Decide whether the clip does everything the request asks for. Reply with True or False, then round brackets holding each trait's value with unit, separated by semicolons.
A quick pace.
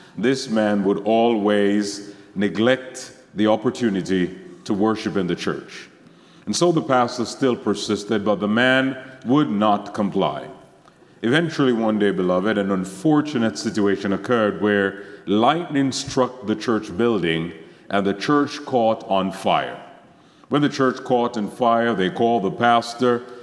False (140 wpm)